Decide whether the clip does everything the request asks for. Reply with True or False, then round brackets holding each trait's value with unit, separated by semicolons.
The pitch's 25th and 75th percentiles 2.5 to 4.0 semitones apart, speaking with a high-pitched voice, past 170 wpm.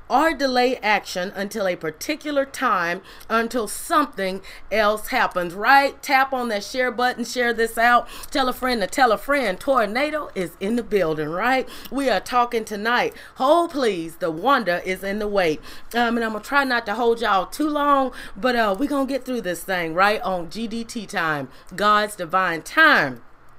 False (5.4 semitones; 230 Hz; 180 wpm)